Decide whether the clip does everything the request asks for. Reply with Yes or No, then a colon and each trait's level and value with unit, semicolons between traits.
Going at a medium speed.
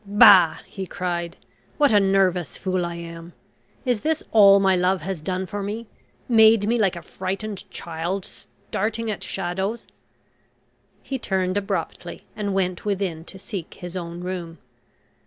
Yes: average, 150 wpm